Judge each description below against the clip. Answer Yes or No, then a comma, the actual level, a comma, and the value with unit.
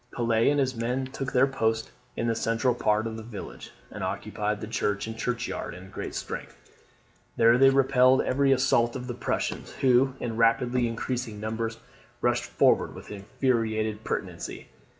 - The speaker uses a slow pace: No, average, 165 wpm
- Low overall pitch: Yes, low, 115 Hz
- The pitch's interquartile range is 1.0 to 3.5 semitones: Yes, narrow, 2.4 semitones